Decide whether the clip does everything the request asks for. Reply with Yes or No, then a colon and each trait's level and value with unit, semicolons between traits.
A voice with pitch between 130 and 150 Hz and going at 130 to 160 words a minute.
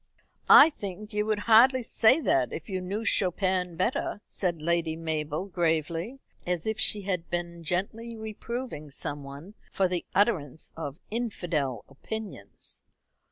No: medium, 180 Hz; average, 140 wpm